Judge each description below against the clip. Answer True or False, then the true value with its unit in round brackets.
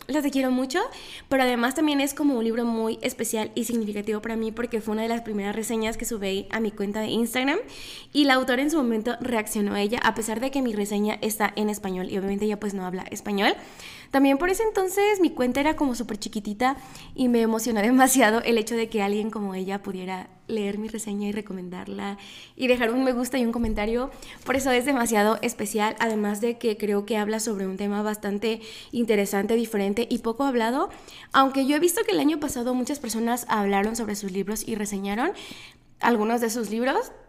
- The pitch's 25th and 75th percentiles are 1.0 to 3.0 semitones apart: False (3.5 semitones)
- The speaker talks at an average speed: False (210 wpm)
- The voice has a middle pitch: False (225 Hz)